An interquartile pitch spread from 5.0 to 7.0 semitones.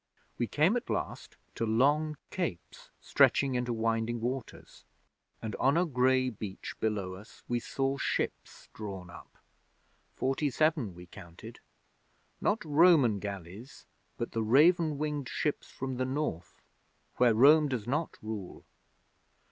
Yes: wide, 5.4 semitones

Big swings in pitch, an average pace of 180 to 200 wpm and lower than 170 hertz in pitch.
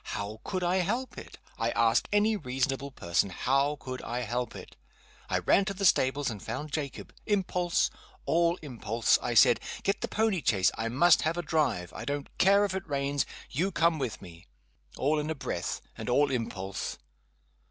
Yes: wide, 6.9 semitones; average, 185 wpm; medium, 140 Hz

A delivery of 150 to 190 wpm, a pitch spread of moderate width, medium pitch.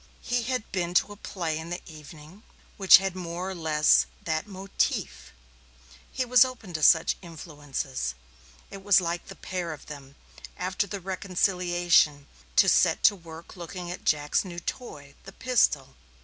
Yes: average, 160 wpm; average, 3.6 semitones; medium, 175 Hz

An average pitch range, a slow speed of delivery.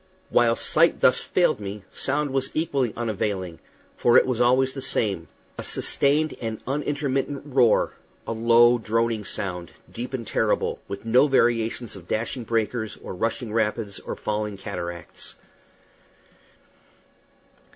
Yes: average, 3.8 semitones; slow, 130 wpm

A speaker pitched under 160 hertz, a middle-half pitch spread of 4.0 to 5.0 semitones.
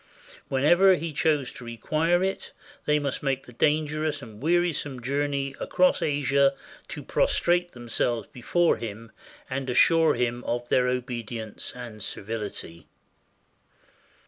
Yes: low, 135 Hz; average, 4.4 semitones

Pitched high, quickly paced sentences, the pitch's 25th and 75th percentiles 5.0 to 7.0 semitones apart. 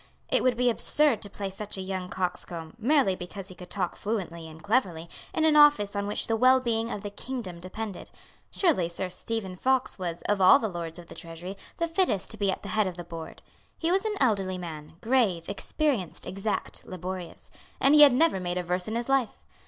Yes: high, 200 Hz; fast, 215 wpm; wide, 5.5 semitones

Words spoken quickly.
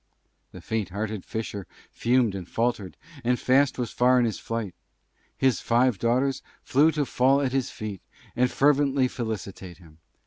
No: average, 160 wpm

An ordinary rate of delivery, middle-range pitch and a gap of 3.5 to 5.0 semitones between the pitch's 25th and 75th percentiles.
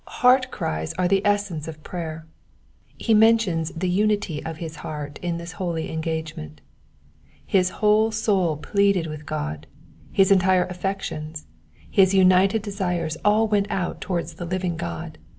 Yes: average, 145 wpm; medium, 180 Hz; average, 3.8 semitones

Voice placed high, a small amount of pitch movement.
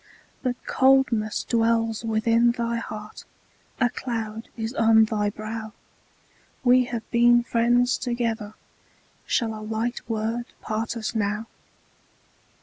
Yes: high, 230 Hz; narrow, 1.7 semitones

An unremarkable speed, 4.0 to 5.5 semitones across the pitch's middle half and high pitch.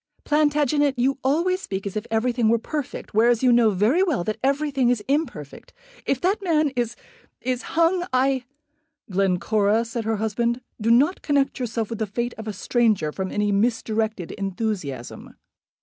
Yes: average, 165 wpm; average, 4.6 semitones; high, 235 Hz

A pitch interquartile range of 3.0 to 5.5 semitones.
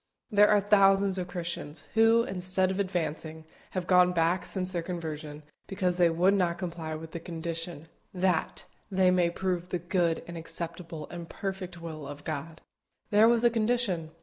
No: narrow, 2.5 semitones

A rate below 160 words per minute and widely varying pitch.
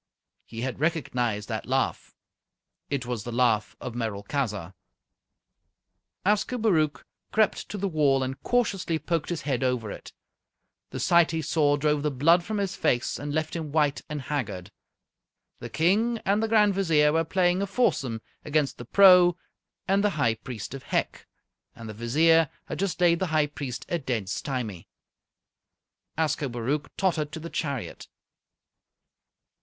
Yes: average, 150 wpm; wide, 5.8 semitones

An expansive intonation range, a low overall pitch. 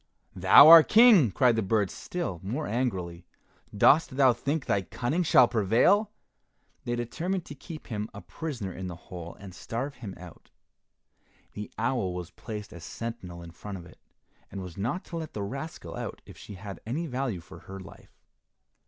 Yes: wide, 6.9 semitones; low, 115 Hz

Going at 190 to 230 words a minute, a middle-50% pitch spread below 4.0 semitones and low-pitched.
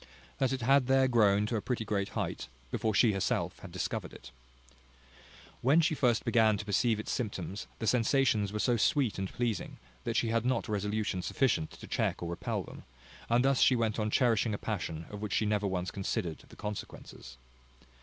Yes: average, 195 wpm; average, 3.3 semitones; low, 110 Hz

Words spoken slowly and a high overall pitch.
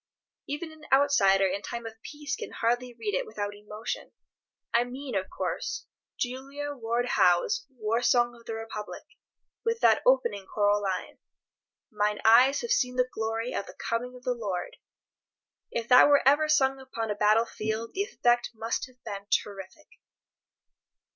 No: average, 160 wpm; high, 235 Hz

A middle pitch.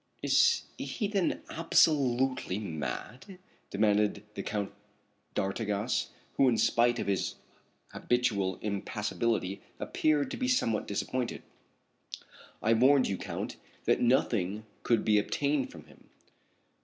No: low, 115 Hz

